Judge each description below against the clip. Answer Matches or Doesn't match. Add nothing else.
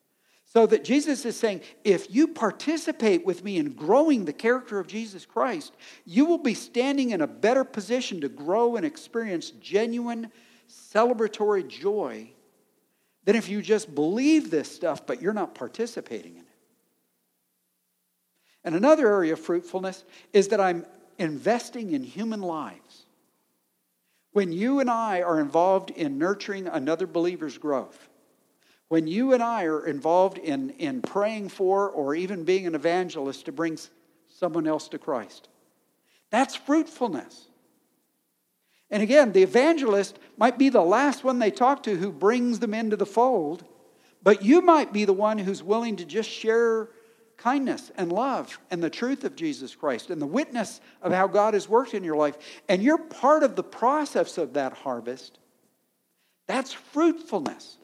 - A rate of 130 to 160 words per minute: Matches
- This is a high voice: Matches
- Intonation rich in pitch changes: Matches